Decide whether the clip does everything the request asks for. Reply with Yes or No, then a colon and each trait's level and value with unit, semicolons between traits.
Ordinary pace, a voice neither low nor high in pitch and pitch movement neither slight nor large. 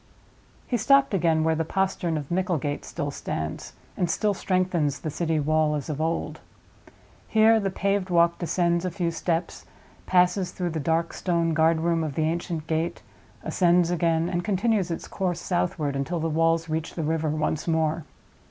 No: average, 170 wpm; medium, 165 Hz; narrow, 2.1 semitones